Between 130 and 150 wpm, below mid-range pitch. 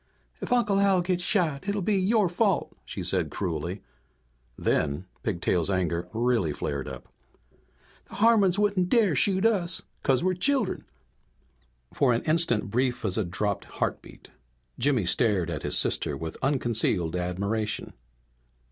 Yes: average, 140 wpm; low, 130 Hz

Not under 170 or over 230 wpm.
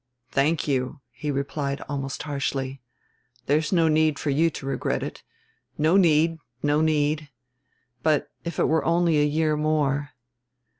No: average, 145 wpm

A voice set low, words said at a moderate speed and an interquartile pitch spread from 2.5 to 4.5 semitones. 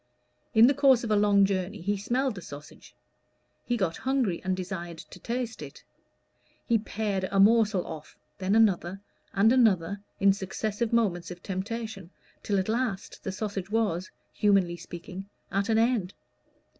No: high, 200 Hz; average, 155 wpm; average, 3.2 semitones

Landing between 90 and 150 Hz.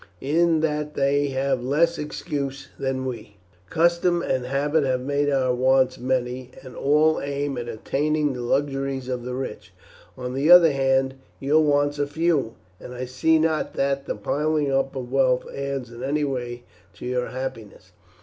Yes: low, 135 Hz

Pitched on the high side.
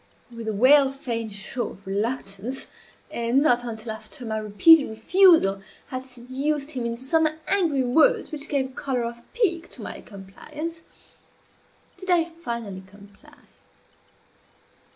Yes: very high, 250 Hz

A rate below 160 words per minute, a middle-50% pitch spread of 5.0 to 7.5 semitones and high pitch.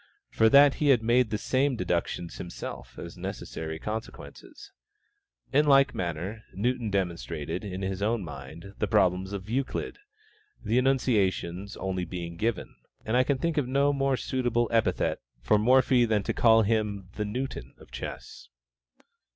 No: average, 150 wpm; wide, 5.4 semitones; low, 110 Hz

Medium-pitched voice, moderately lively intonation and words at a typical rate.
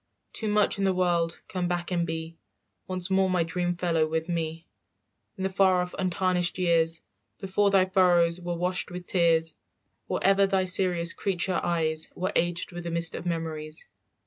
No: medium, 175 Hz; narrow, 1.9 semitones; average, 175 wpm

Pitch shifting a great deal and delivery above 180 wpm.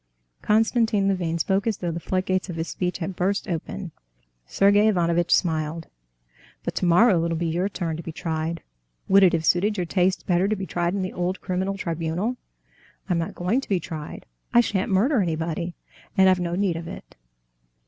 No: average, 2.8 semitones; average, 190 wpm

